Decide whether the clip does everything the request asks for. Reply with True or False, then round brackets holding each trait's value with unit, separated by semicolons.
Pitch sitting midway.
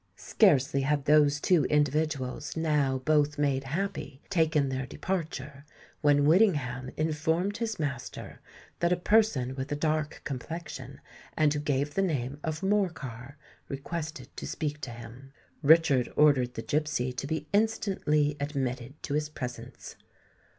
True (150 Hz)